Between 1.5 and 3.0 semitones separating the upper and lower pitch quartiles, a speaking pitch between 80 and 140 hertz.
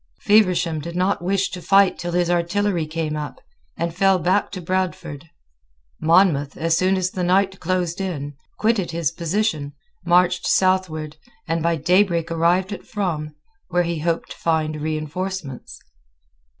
No: average, 2.7 semitones; medium, 175 Hz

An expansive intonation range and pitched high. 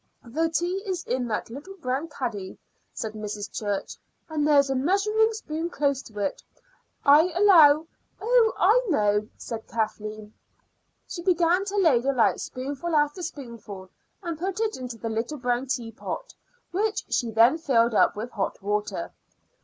Yes: wide, 7.3 semitones; very high, 275 Hz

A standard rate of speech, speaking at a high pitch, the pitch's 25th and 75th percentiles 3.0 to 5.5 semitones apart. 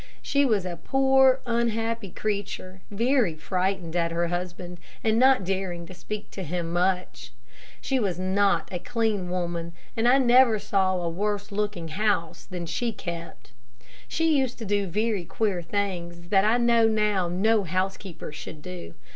Yes: average, 160 wpm; high, 195 Hz; average, 4.3 semitones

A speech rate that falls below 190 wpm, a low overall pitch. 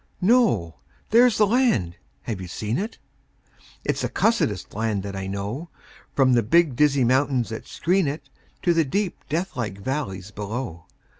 Yes: average, 155 wpm; low, 130 Hz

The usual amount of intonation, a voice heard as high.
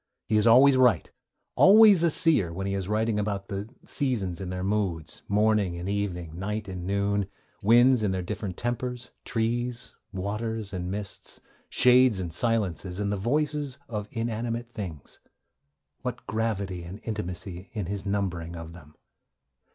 No: average, 3.8 semitones; low, 105 Hz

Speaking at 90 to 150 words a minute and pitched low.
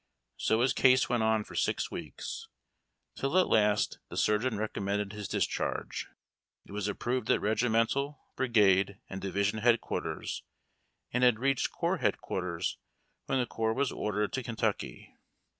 Yes: average, 140 wpm; low, 110 Hz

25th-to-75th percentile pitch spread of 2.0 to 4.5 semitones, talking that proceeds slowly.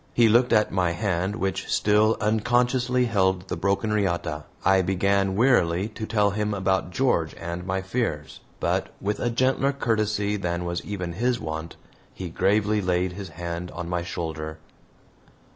No: average, 3.7 semitones; average, 160 wpm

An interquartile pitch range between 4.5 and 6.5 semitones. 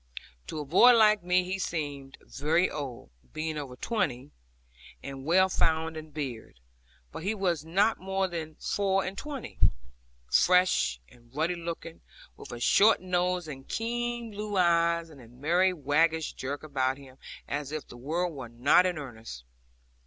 Yes: average, 4.8 semitones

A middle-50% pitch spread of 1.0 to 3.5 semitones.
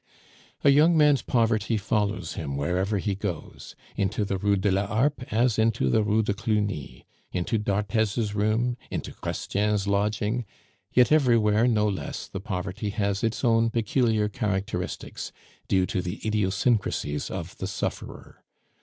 Yes: narrow, 2.6 semitones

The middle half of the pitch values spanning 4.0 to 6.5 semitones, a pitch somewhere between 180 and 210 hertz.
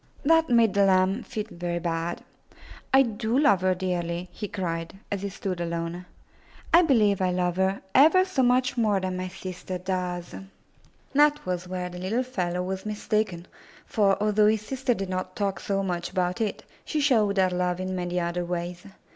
No: average, 3.3 semitones; high, 190 Hz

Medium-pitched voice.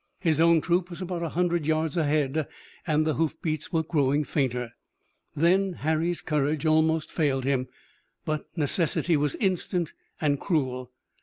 Yes: medium, 155 Hz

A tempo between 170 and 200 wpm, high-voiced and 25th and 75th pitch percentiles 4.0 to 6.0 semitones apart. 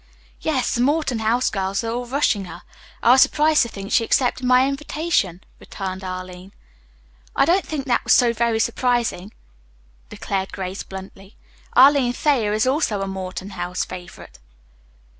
No: average, 155 wpm; high, 225 Hz; average, 5.1 semitones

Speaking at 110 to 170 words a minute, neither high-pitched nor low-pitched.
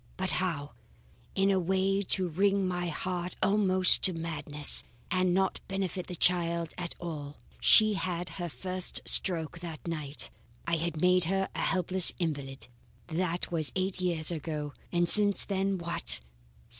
Yes: average, 150 wpm; medium, 175 Hz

